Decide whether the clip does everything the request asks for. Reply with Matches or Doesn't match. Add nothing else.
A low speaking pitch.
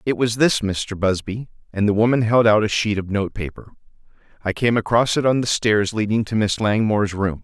Matches